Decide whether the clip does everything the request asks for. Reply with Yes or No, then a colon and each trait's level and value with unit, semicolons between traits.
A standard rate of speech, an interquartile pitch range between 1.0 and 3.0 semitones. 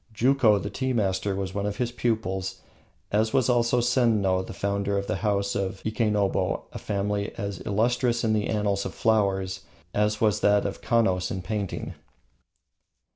Yes: average, 170 wpm; narrow, 2.4 semitones